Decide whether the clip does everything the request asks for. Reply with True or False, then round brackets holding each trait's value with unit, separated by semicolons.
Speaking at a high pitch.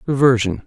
False (125 Hz)